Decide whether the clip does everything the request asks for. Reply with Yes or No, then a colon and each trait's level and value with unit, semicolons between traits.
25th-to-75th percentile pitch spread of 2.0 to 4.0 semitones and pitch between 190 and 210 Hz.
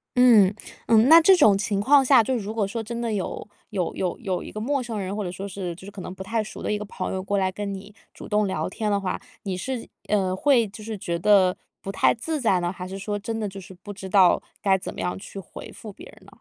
Yes: average, 2.9 semitones; high, 200 Hz